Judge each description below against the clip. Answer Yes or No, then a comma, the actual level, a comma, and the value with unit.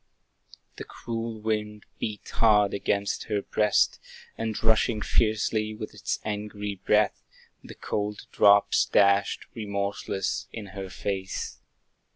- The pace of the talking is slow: Yes, slow, 115 wpm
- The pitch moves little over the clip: Yes, narrow, 1.3 semitones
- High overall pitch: No, low, 105 Hz